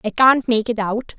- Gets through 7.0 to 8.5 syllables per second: No, 4.7 syllables/s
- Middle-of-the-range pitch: No, high, 225 Hz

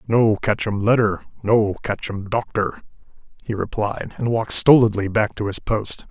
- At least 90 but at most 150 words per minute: Yes, average, 145 wpm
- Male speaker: Yes, male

